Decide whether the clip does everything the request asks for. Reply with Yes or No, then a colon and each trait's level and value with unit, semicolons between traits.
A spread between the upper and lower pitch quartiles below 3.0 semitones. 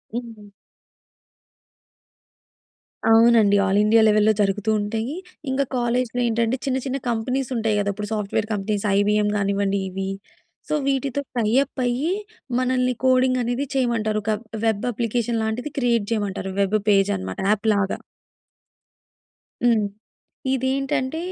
No: average, 3.4 semitones